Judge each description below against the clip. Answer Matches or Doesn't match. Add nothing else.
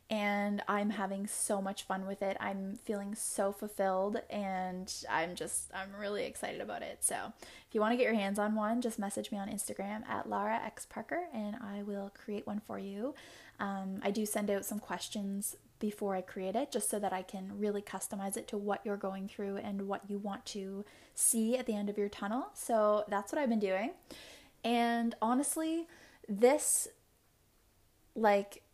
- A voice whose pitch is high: Matches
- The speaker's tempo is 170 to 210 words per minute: Matches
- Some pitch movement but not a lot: Doesn't match